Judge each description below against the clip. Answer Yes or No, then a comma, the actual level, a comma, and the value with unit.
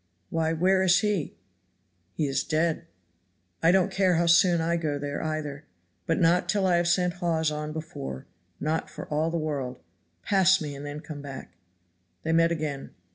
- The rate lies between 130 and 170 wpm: No, average, 180 wpm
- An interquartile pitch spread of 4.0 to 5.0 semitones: No, narrow, 2.6 semitones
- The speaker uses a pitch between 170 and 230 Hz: No, medium, 160 Hz